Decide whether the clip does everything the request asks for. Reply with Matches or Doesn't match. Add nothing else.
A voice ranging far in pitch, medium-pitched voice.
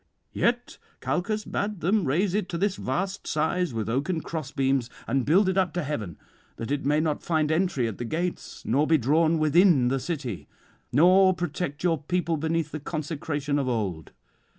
Doesn't match